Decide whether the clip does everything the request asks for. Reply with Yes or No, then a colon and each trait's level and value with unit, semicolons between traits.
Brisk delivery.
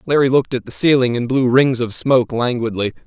Yes: fast, 215 wpm